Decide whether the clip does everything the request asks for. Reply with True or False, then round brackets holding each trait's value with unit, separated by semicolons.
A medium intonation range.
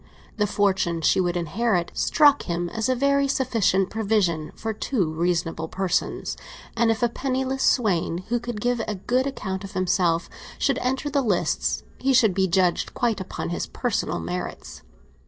False (5.8 semitones)